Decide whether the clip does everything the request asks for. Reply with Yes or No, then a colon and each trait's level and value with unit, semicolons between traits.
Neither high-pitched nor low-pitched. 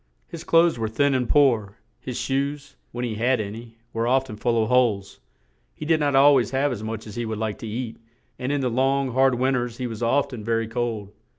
No: low, 120 Hz